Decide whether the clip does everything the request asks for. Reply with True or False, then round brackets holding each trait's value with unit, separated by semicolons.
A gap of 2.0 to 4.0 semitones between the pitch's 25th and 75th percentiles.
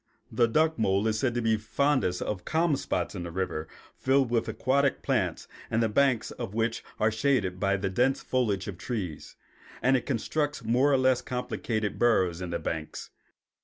False (5.3 semitones)